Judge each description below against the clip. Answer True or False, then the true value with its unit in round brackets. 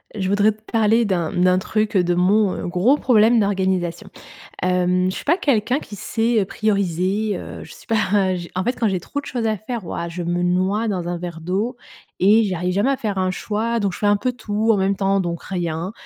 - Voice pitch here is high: True (200 Hz)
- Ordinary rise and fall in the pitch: True (3.3 semitones)